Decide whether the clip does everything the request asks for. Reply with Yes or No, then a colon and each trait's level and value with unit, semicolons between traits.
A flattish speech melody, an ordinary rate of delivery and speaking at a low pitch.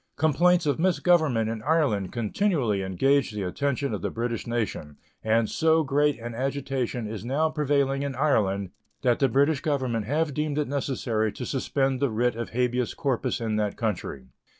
No: average, 4.3 semitones; average, 170 wpm; low, 130 Hz